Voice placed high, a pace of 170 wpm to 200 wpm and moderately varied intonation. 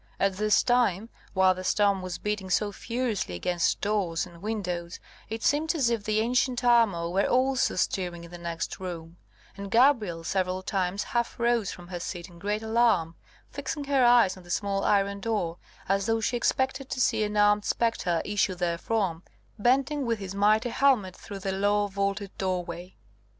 Yes: high, 200 Hz; average, 175 wpm; average, 4.1 semitones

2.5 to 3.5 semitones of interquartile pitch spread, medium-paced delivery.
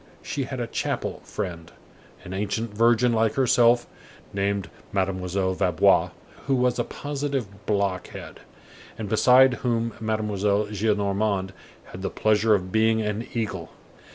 No: average, 3.1 semitones; slow, 125 wpm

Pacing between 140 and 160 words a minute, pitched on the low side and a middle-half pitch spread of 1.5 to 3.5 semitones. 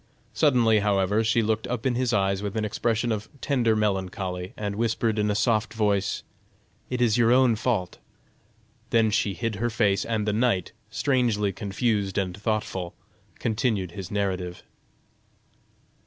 Yes: average, 150 wpm; low, 105 Hz; average, 2.7 semitones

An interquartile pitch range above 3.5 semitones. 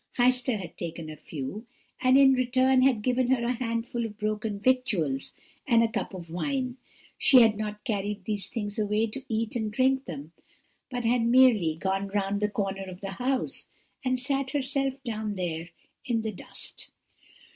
Yes: average, 4.3 semitones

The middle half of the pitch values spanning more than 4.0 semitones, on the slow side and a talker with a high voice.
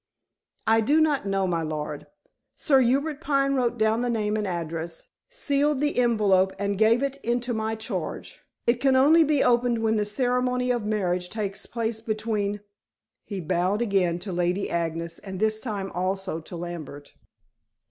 No: average, 5.0 semitones; average, 170 wpm; high, 215 Hz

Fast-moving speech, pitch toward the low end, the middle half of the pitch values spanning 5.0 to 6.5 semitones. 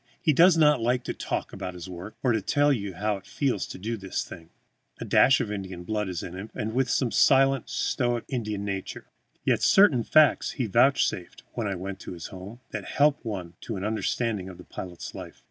Yes: fast, 215 wpm; low, 110 Hz; average, 5.3 semitones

